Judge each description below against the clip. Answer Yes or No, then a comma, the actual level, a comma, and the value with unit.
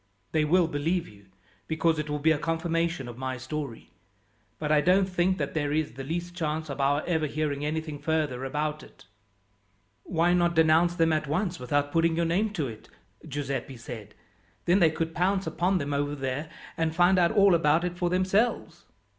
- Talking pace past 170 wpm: Yes, average, 190 wpm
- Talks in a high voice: No, medium, 160 Hz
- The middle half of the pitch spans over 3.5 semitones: No, average, 3.2 semitones